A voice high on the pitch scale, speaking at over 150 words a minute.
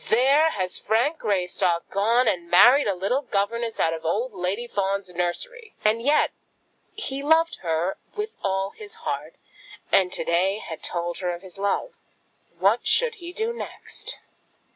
Yes: high, 205 Hz; average, 165 wpm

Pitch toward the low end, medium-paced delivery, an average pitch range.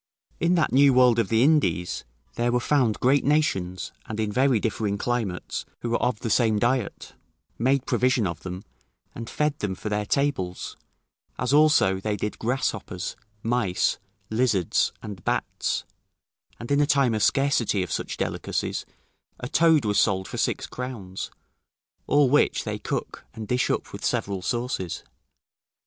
Yes: low, 120 Hz; average, 160 wpm; average, 4.7 semitones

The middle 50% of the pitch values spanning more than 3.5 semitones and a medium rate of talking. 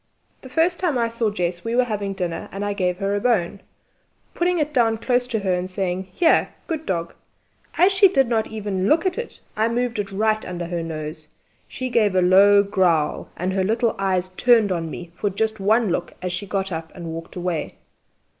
No: average, 4.4 semitones; fast, 210 wpm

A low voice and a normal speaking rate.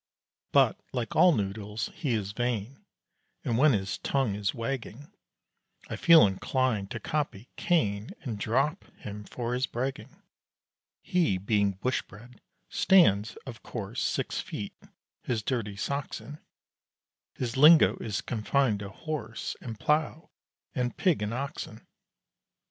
No: low, 120 Hz; slow, 130 wpm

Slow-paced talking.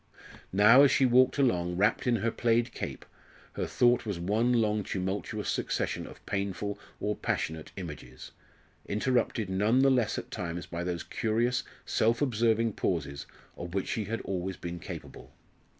No: average, 155 wpm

